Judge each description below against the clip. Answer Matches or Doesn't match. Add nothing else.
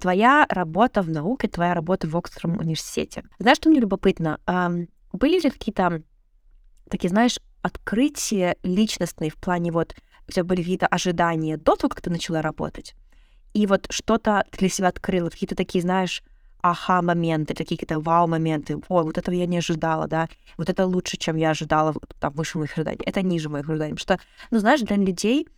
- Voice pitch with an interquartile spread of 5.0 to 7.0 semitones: Doesn't match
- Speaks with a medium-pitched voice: Matches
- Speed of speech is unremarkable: Doesn't match